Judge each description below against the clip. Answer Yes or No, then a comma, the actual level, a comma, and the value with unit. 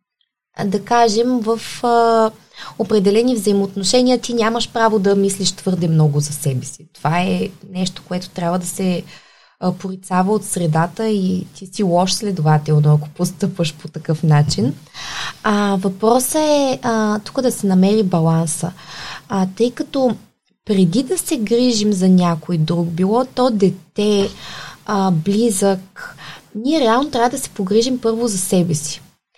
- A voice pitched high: Yes, high, 200 Hz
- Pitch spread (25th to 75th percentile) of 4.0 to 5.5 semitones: Yes, average, 4.4 semitones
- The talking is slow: No, average, 145 wpm